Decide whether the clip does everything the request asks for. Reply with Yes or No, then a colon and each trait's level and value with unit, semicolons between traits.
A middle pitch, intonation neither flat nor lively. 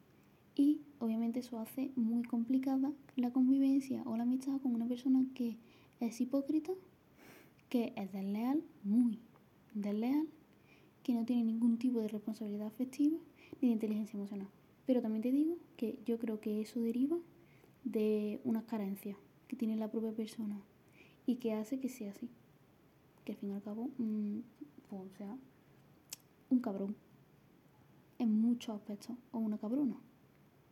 No: high, 235 Hz; average, 3.1 semitones